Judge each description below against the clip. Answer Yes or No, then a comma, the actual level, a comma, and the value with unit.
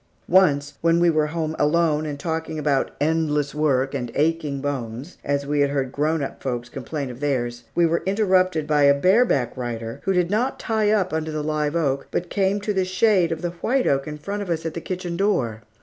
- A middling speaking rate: No, fast, 220 wpm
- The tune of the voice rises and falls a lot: No, average, 4.0 semitones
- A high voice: No, medium, 155 Hz